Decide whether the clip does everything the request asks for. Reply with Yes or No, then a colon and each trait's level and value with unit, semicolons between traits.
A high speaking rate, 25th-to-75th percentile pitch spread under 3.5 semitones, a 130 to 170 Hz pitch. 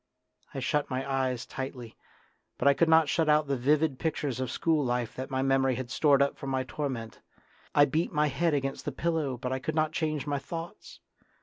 Yes: fast, 210 wpm; average, 2.8 semitones; medium, 140 Hz